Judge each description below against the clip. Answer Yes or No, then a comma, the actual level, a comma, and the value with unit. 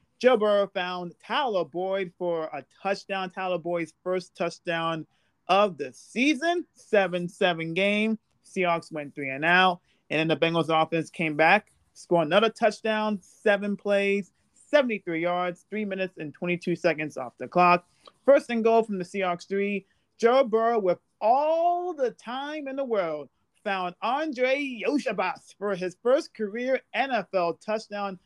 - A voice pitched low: No, high, 190 Hz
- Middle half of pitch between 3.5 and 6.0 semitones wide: Yes, average, 4.2 semitones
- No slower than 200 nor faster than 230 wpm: No, average, 150 wpm